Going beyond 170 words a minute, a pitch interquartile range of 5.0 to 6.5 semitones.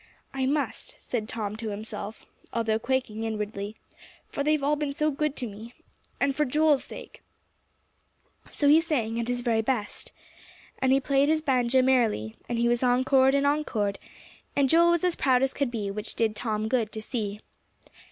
No: average, 180 wpm; average, 4.3 semitones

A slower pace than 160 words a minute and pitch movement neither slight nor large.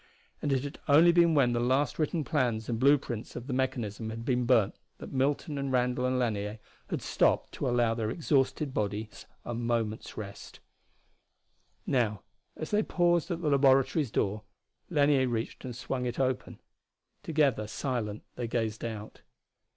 No: average, 165 wpm; average, 3.9 semitones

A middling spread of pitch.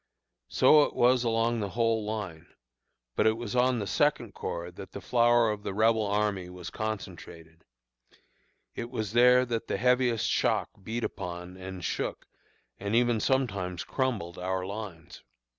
Yes: average, 4.3 semitones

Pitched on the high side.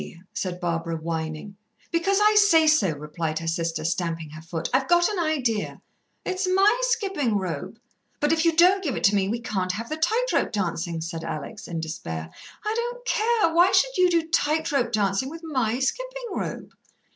Yes: very high, 255 Hz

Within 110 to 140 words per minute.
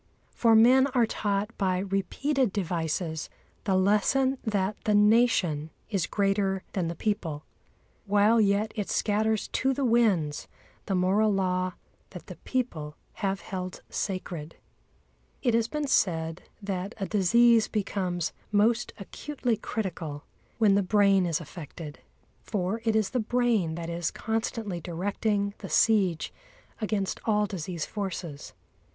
Yes: slow, 135 wpm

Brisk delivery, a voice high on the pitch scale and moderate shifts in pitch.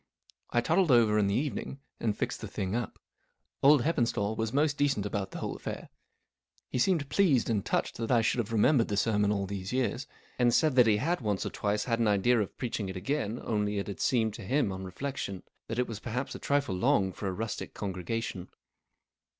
No: fast, 210 wpm; low, 115 Hz; average, 4.2 semitones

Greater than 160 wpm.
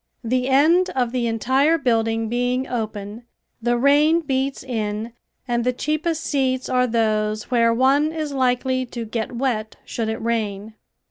No: average, 150 wpm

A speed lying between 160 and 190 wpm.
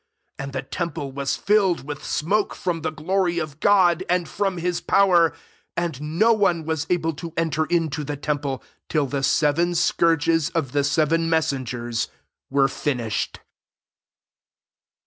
No: average, 145 wpm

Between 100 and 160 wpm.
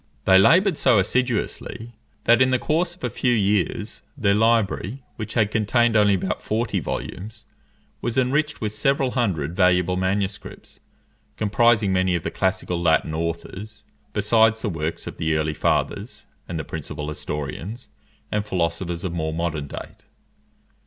Yes: average, 150 wpm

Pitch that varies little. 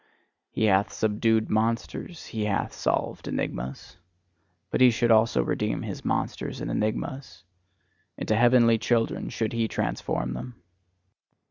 Yes: narrow, 1.8 semitones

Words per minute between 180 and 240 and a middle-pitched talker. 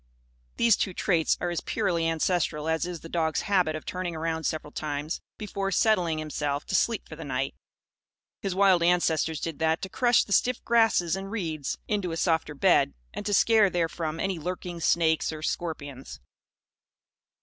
No: average, 170 wpm; medium, 170 Hz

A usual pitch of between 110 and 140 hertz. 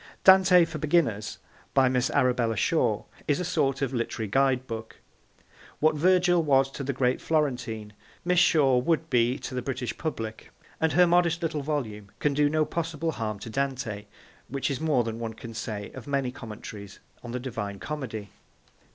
Yes: low, 135 Hz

